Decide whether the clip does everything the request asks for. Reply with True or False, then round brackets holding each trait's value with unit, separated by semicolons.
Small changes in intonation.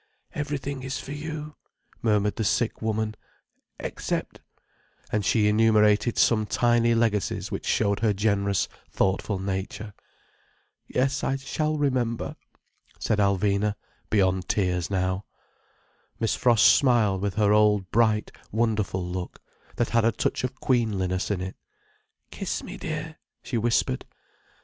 False (3.1 semitones)